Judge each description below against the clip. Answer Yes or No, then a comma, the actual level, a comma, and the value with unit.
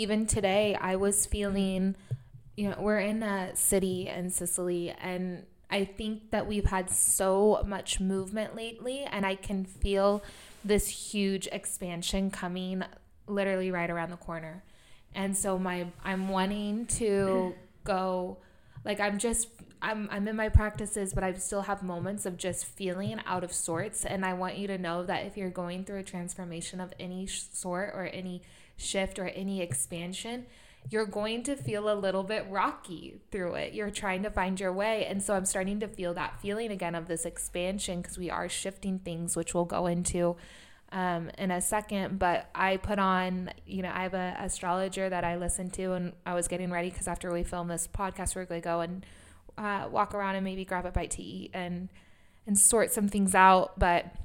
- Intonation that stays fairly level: Yes, narrow, 2.0 semitones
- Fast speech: No, average, 190 wpm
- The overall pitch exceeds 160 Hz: Yes, high, 190 Hz